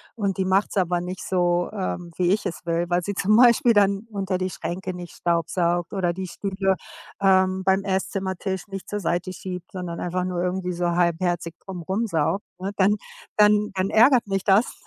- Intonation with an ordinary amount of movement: No, narrow, 2.0 semitones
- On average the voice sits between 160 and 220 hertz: Yes, medium, 185 Hz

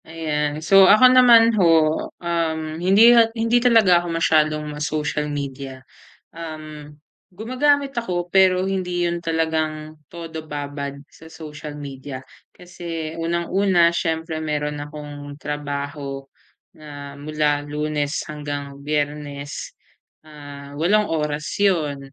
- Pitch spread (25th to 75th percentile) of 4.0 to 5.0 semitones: No, average, 3.0 semitones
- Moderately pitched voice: Yes, medium, 155 Hz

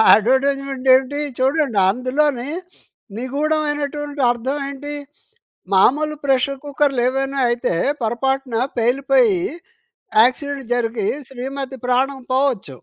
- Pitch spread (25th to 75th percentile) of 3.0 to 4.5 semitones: No, narrow, 2.4 semitones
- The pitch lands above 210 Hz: Yes, very high, 270 Hz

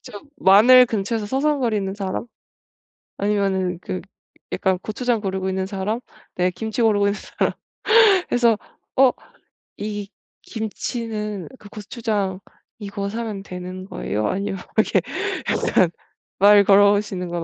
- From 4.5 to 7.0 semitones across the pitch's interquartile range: No, narrow, 2.5 semitones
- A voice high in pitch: Yes, high, 205 Hz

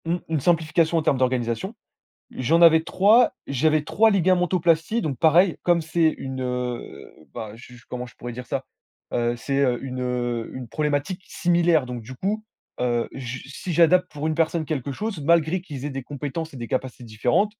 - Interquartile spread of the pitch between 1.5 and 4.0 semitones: No, average, 5.3 semitones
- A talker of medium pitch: Yes, medium, 150 Hz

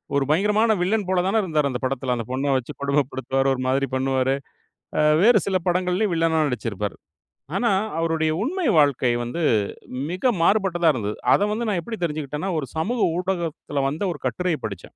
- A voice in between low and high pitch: Yes, medium, 160 Hz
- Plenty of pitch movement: Yes, wide, 5.9 semitones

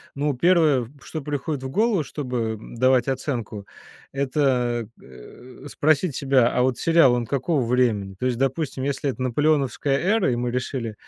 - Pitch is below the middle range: Yes, low, 130 Hz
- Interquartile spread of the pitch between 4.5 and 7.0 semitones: No, average, 3.2 semitones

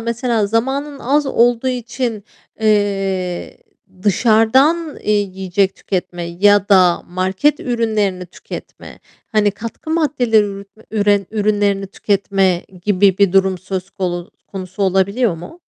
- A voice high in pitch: Yes, high, 205 Hz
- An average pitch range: Yes, average, 3.5 semitones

